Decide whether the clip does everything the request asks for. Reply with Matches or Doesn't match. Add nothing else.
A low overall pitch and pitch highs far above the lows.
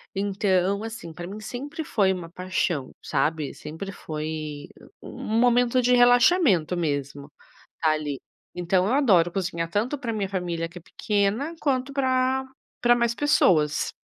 Doesn't match